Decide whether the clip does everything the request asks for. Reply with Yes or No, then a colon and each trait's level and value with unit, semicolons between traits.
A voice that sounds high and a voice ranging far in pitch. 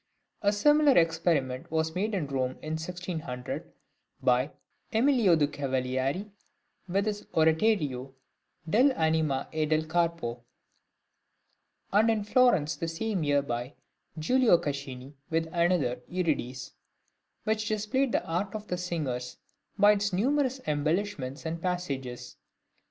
No: medium, 165 Hz; wide, 6.5 semitones